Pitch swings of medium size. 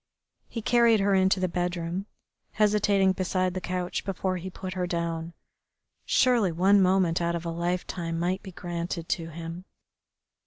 No: narrow, 2.2 semitones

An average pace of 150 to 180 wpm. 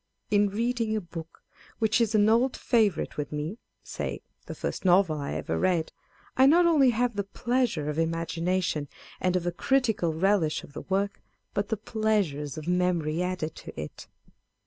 Yes: average, 175 wpm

